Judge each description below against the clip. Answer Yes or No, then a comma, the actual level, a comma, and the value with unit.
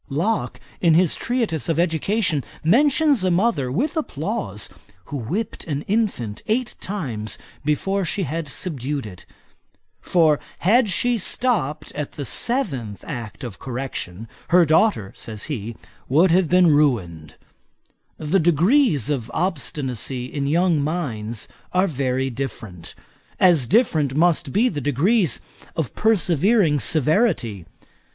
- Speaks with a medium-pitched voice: Yes, medium, 155 Hz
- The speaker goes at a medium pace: No, slow, 125 wpm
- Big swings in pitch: Yes, wide, 6.7 semitones